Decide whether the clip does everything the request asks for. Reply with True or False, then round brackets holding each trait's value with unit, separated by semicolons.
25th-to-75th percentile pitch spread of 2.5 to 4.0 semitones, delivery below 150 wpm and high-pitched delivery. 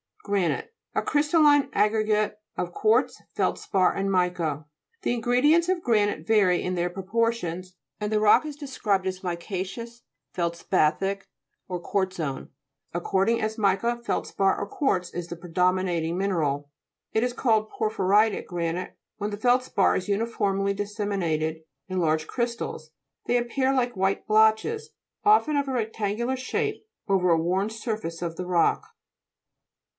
False (4.5 semitones; 140 wpm; 200 Hz)